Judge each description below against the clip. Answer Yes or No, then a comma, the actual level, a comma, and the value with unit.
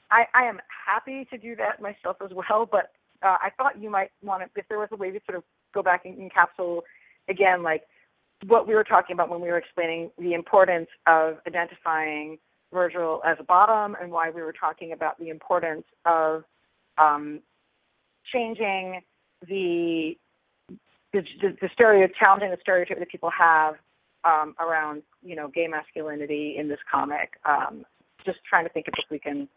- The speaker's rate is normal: Yes, average, 180 wpm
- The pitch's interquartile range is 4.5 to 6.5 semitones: No, average, 3.4 semitones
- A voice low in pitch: No, medium, 175 Hz